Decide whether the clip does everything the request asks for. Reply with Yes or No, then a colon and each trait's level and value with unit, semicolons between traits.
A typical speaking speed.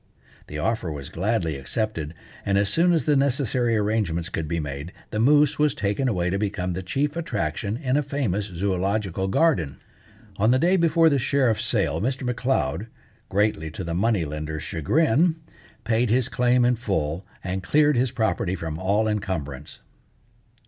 Yes: average, 165 wpm